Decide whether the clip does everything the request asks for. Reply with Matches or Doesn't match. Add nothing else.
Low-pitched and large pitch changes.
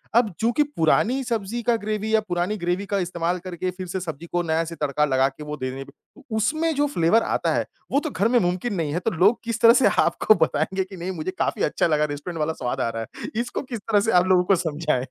Doesn't match